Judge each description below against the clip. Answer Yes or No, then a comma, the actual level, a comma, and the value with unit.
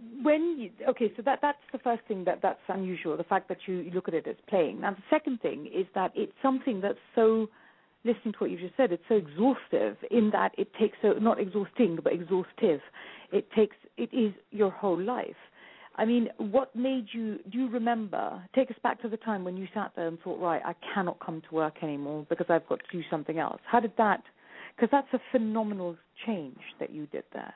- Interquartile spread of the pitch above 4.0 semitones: Yes, average, 4.7 semitones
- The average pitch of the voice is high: Yes, high, 215 Hz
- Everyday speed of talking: No, fast, 225 wpm